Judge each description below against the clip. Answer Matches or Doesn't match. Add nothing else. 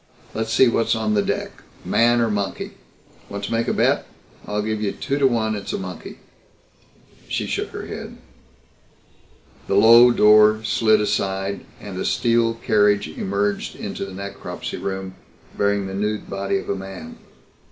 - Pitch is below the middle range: Matches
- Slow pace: Doesn't match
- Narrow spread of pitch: Matches